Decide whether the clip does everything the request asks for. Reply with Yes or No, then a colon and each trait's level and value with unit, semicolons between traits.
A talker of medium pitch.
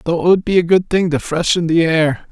Yes: medium, 170 Hz